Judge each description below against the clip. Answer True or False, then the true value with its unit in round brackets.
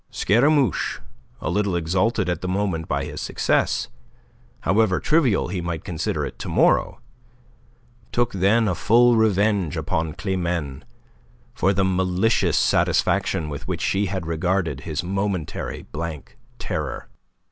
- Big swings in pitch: False (3.7 semitones)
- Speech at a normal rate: False (130 wpm)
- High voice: False (95 Hz)